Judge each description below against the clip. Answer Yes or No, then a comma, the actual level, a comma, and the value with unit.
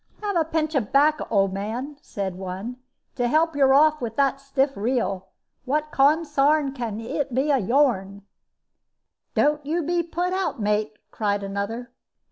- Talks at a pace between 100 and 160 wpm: Yes, average, 155 wpm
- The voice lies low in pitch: No, very high, 270 Hz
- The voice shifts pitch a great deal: Yes, wide, 6.0 semitones